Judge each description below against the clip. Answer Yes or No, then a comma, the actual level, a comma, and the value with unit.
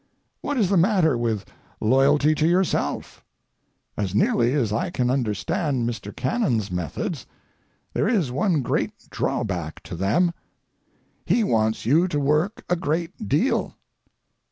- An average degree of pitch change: No, wide, 8.0 semitones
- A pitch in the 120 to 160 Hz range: Yes, medium, 140 Hz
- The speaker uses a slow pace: Yes, slow, 130 wpm